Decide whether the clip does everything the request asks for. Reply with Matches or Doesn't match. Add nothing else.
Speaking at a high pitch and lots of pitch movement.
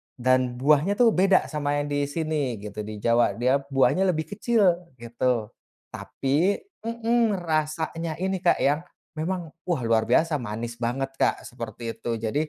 Doesn't match